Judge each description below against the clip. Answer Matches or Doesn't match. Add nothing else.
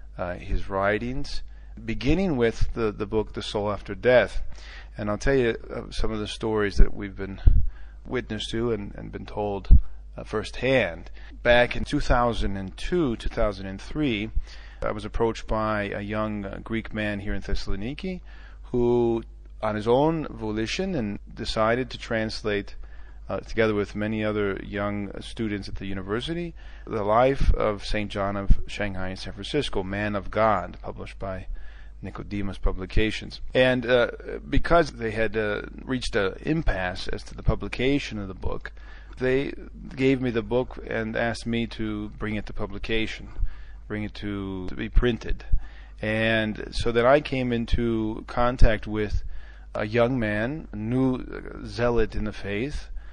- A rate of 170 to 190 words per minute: Doesn't match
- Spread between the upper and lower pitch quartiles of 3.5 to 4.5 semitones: Doesn't match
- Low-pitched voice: Matches